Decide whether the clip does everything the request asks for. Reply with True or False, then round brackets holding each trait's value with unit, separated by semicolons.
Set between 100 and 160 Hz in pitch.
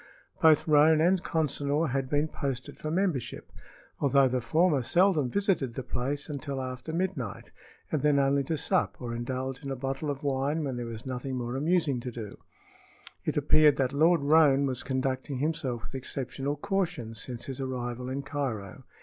True (140 Hz)